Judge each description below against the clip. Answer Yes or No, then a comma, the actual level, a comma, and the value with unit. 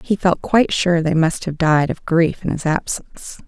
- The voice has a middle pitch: Yes, medium, 170 Hz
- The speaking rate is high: Yes, fast, 225 wpm